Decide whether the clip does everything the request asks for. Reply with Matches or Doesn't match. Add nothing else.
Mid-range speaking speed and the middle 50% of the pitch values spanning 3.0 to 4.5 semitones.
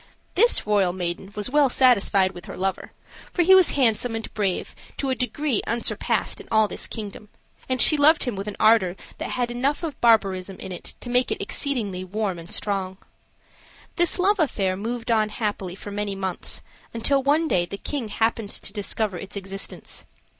Doesn't match